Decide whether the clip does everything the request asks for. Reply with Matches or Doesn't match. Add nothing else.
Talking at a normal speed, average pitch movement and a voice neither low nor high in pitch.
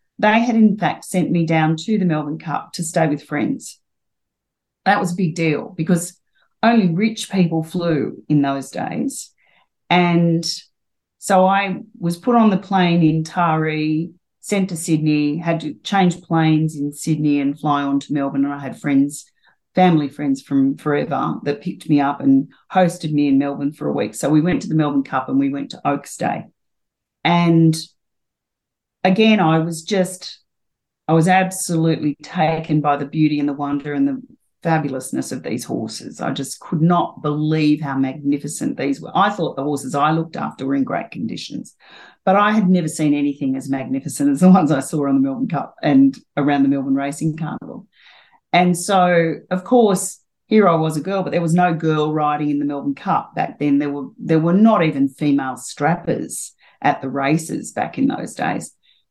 Matches